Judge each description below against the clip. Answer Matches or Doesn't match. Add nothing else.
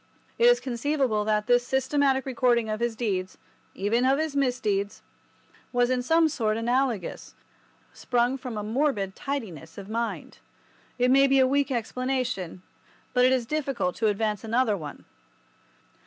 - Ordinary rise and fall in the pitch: Matches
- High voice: Matches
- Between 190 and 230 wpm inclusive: Doesn't match